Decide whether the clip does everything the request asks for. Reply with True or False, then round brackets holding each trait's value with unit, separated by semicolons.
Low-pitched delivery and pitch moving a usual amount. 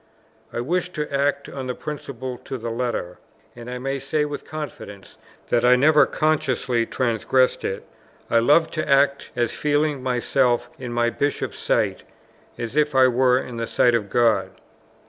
True (130 Hz; 3.3 semitones)